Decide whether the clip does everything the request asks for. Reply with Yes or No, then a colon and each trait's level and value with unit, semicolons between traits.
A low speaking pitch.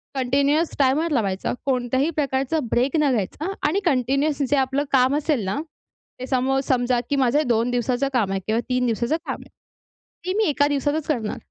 No: very high, 265 Hz